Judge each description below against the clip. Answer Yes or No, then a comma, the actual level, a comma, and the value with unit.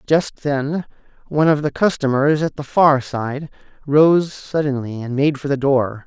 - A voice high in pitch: No, medium, 145 Hz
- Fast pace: No, average, 170 wpm